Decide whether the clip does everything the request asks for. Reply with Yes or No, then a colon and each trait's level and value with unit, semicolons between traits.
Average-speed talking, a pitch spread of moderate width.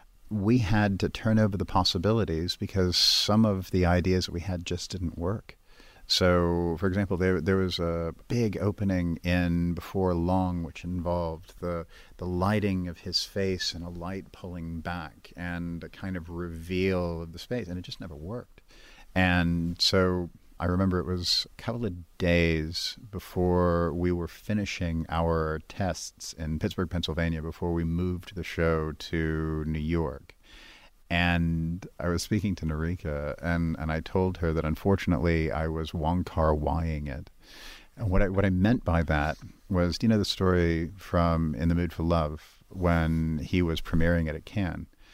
No: average, 170 wpm; narrow, 2.1 semitones